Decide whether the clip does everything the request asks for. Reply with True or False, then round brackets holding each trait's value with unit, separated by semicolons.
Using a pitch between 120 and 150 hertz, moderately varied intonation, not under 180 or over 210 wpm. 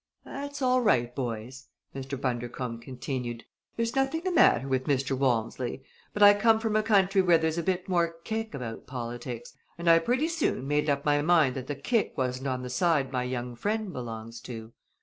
False (140 Hz; 8.1 semitones; 190 wpm)